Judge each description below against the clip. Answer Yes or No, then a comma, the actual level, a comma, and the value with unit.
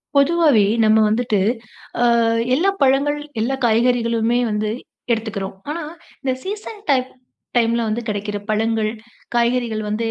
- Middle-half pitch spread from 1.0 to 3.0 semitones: No, average, 3.8 semitones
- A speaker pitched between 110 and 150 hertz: No, high, 235 Hz